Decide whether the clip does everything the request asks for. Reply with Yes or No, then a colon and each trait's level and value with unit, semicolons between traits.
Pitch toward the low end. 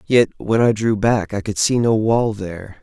Yes: low, 105 Hz